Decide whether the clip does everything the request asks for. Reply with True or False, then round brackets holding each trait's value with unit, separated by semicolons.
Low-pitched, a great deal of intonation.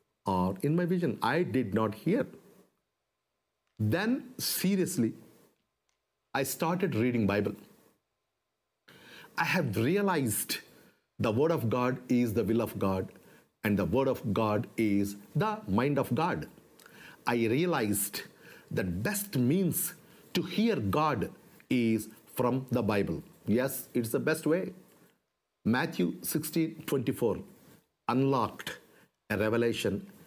True (125 Hz; 7.2 semitones)